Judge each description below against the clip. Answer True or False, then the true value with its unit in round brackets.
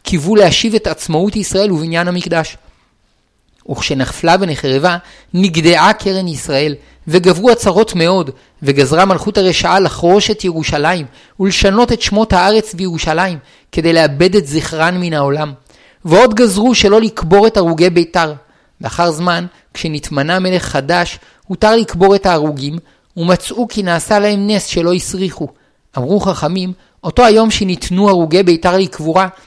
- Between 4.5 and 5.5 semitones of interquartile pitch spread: False (3.5 semitones)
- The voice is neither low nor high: True (180 Hz)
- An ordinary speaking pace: True (130 wpm)